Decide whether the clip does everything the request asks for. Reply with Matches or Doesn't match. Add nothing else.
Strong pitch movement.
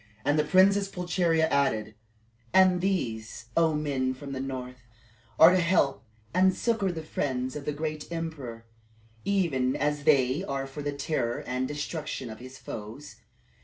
Doesn't match